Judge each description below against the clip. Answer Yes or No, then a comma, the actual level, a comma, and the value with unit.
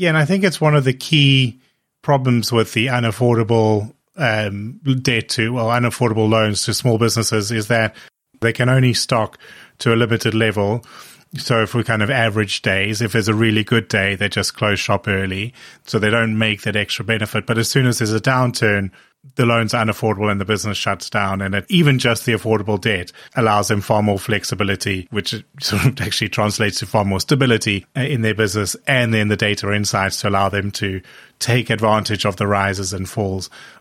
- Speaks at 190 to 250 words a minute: Yes, average, 200 wpm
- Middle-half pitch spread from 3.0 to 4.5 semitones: No, narrow, 2.5 semitones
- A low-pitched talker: Yes, low, 110 Hz